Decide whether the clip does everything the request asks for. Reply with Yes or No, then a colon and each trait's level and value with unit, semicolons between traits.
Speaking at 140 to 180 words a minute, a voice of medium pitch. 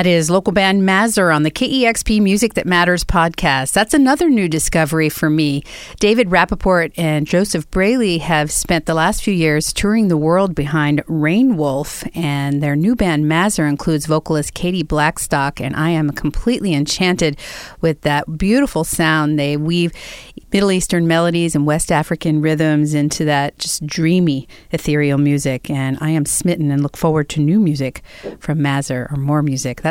Yes: average, 165 wpm; medium, 160 Hz